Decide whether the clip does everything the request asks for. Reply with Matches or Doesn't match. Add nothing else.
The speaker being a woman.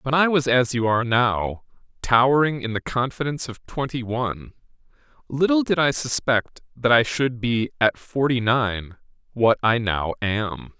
Doesn't match